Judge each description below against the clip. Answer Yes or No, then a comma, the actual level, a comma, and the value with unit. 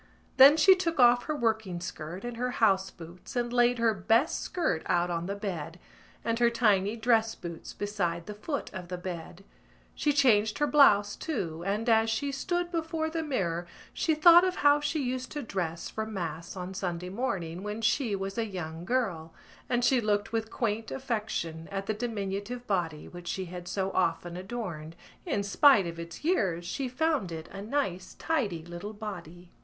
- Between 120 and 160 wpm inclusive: No, average, 185 wpm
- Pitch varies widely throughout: Yes, wide, 5.7 semitones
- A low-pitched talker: No, high, 210 Hz